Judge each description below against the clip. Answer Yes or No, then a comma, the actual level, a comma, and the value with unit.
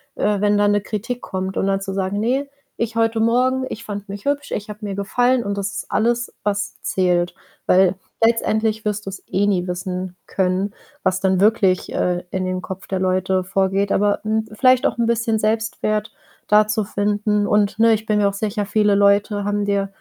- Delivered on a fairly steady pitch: Yes, narrow, 2.2 semitones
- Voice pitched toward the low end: No, high, 205 Hz